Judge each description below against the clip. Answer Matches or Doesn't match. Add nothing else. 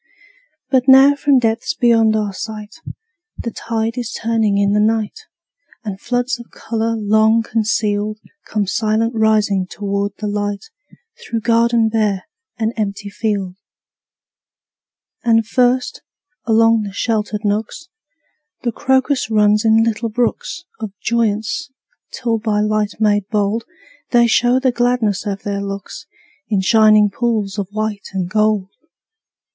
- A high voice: Matches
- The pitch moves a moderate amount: Doesn't match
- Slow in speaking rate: Matches